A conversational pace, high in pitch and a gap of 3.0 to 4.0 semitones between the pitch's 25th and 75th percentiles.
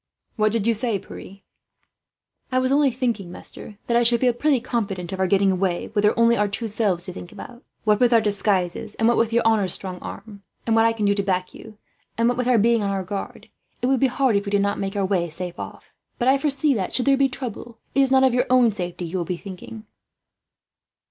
No: fast, 250 wpm; high, 220 Hz; average, 3.7 semitones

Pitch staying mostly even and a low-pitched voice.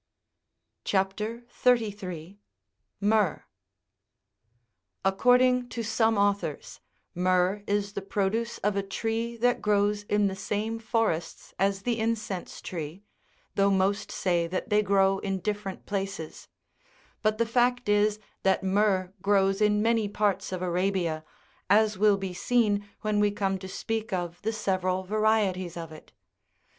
No: narrow, 2.2 semitones; high, 200 Hz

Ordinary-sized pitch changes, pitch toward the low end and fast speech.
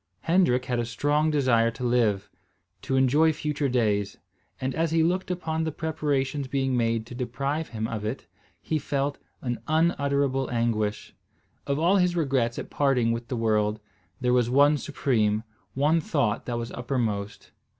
No: average, 4.2 semitones; low, 130 Hz; average, 160 wpm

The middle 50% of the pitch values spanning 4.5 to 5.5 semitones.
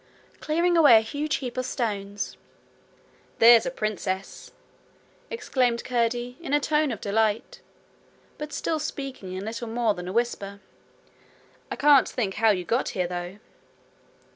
Yes: average, 5.2 semitones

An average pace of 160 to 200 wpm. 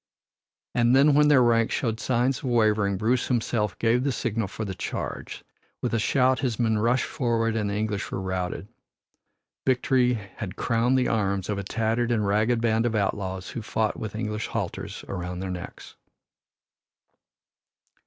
Yes: average, 165 wpm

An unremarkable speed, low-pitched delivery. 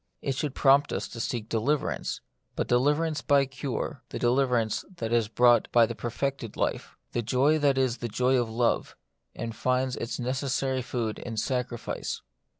Yes: average, 165 wpm; low, 125 Hz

